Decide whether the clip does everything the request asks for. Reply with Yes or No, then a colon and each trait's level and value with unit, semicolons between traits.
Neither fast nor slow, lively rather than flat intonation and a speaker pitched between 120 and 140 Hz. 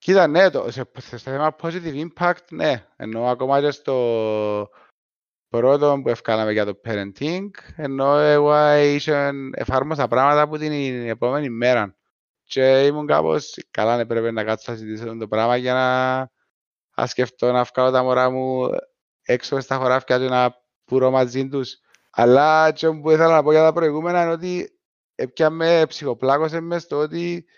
No: average, 160 wpm; average, 4.0 semitones; low, 135 Hz